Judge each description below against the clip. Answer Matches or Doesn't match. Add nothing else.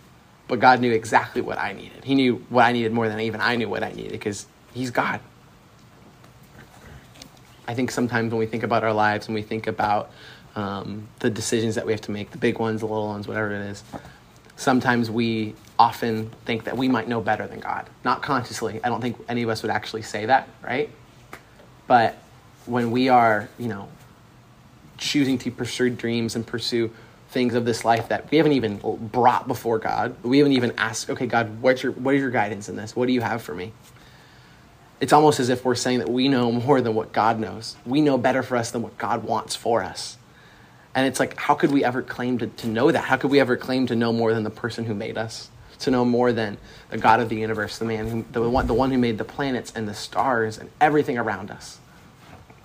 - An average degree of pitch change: Doesn't match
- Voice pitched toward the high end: Doesn't match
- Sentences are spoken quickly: Matches